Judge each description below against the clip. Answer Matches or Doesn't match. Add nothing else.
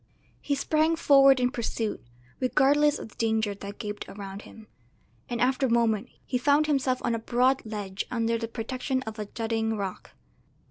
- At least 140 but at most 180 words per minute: Matches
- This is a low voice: Doesn't match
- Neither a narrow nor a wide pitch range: Matches